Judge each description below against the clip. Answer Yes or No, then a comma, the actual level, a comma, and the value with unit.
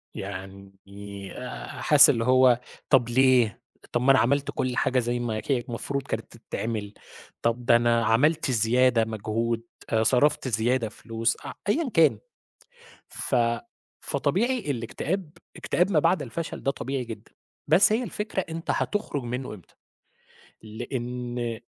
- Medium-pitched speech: No, low, 120 Hz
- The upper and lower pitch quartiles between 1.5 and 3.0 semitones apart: No, average, 3.7 semitones